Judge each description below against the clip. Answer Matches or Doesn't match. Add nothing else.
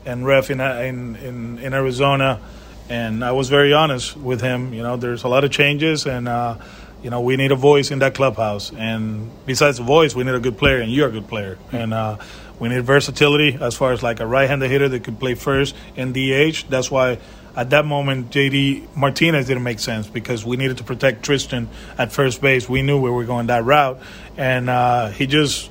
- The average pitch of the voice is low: Matches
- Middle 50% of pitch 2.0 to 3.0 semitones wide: Matches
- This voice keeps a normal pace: Doesn't match